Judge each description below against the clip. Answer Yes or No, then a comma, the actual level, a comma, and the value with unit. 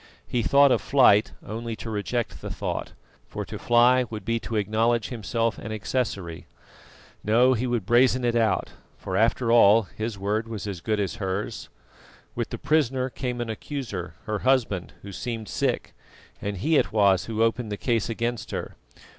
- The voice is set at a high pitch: No, low, 115 Hz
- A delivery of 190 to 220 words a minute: No, average, 175 wpm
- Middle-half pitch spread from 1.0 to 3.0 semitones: Yes, narrow, 2.6 semitones